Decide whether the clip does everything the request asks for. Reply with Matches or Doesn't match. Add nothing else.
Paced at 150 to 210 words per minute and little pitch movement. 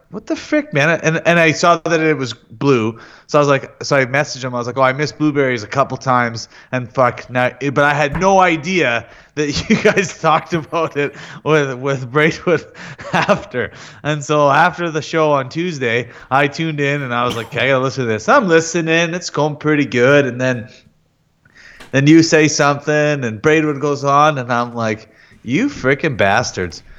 Doesn't match